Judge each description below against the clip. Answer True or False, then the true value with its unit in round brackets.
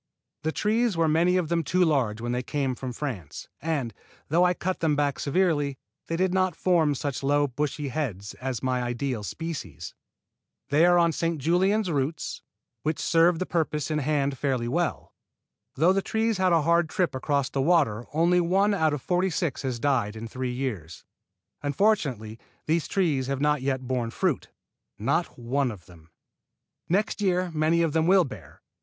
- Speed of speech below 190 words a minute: True (180 wpm)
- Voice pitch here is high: False (150 Hz)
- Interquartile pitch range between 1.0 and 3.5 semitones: False (4.9 semitones)